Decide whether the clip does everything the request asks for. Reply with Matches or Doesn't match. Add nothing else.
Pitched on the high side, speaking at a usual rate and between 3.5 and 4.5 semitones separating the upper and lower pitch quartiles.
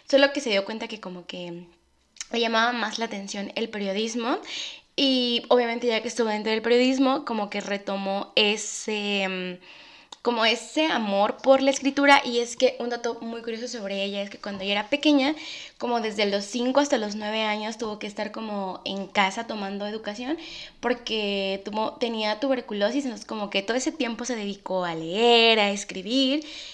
Matches